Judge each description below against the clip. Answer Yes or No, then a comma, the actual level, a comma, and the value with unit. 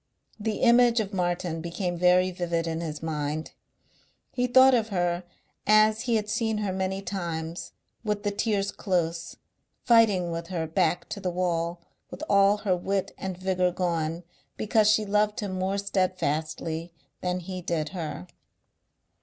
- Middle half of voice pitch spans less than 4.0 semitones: Yes, average, 3.5 semitones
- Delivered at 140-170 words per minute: Yes, average, 155 wpm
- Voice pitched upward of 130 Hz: Yes, medium, 185 Hz